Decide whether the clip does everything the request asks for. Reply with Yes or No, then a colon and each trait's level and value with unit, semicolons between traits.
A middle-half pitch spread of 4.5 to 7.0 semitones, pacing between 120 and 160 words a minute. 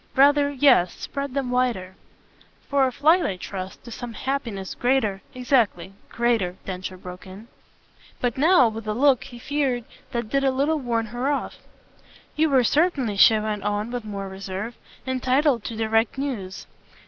No: average, 4.8 semitones; average, 170 wpm